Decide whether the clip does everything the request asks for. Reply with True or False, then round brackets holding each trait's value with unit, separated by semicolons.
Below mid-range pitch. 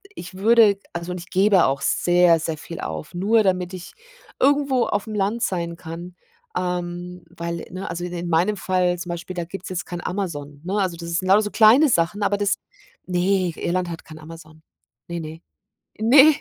False (180 Hz)